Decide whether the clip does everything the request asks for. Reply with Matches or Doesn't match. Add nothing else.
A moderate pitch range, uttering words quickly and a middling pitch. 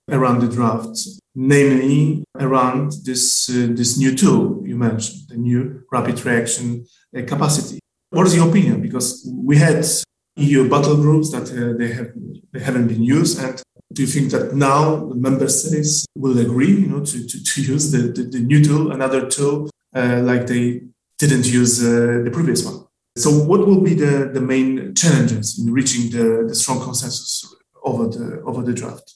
Doesn't match